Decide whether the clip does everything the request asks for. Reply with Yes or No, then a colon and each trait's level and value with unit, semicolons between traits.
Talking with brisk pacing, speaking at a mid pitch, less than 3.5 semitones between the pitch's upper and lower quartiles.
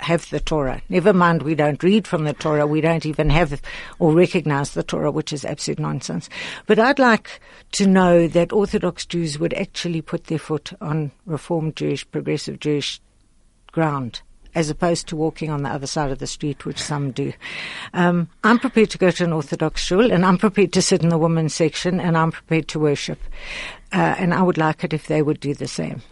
Yes: fast, 210 wpm; medium, 160 Hz; average, 3.1 semitones